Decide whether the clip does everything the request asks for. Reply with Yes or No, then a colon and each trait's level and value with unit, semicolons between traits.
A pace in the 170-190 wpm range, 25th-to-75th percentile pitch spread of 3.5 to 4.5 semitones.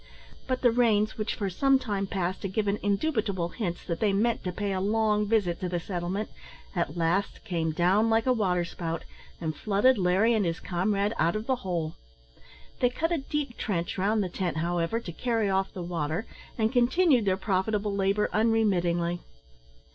Yes: average, 180 wpm; average, 4.1 semitones